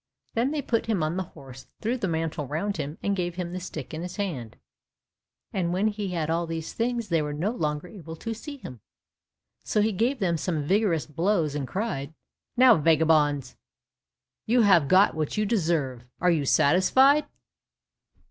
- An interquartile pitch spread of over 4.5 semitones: Yes, wide, 5.4 semitones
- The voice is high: No, medium, 175 Hz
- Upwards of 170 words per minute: Yes, average, 180 wpm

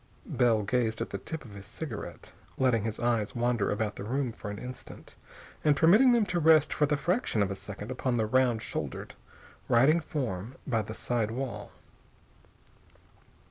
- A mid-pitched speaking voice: No, low, 120 Hz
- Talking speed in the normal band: Yes, average, 175 wpm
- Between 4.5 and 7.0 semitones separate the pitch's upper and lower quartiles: Yes, average, 4.8 semitones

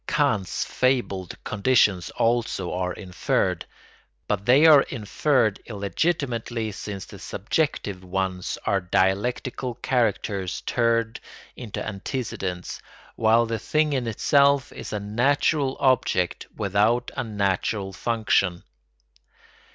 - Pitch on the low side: Yes, low, 110 Hz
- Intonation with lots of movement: No, average, 4.7 semitones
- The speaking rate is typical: No, slow, 105 wpm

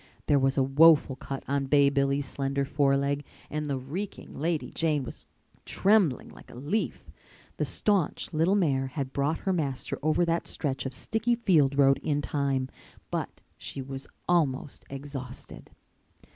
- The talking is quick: No, average, 155 wpm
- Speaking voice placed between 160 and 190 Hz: No, medium, 140 Hz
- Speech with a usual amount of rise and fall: Yes, average, 3.1 semitones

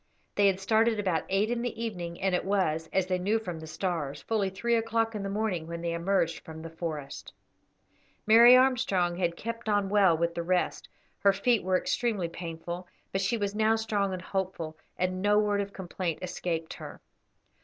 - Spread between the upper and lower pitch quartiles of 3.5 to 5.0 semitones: Yes, average, 4.0 semitones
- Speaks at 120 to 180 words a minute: No, average, 195 wpm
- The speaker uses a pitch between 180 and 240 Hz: Yes, high, 190 Hz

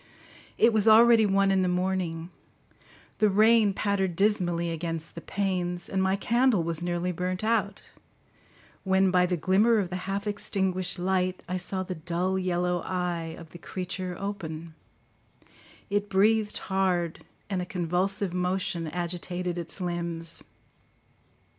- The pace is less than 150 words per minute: Yes, average, 140 wpm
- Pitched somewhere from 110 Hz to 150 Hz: No, medium, 185 Hz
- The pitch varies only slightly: Yes, narrow, 2.1 semitones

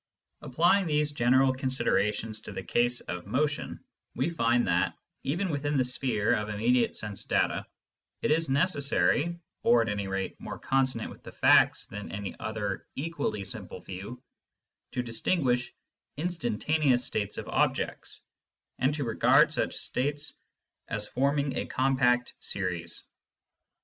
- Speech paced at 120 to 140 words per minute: Yes, slow, 135 wpm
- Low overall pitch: Yes, low, 125 Hz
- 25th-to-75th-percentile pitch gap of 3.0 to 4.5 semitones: No, average, 5.3 semitones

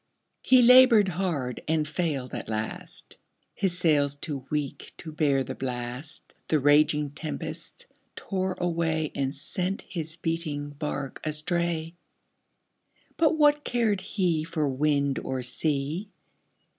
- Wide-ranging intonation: No, average, 4.0 semitones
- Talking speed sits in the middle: No, slow, 120 wpm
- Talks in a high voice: No, medium, 155 Hz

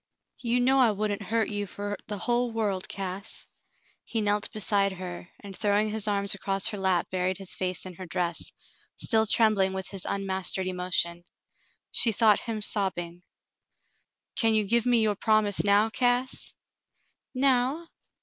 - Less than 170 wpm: Yes, average, 160 wpm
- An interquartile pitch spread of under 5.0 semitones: Yes, average, 2.8 semitones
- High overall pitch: Yes, high, 205 Hz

